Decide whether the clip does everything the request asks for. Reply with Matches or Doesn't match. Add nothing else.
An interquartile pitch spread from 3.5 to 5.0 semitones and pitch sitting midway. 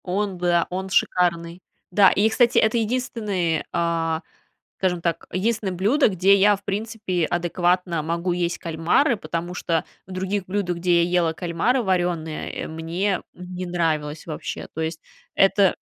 Doesn't match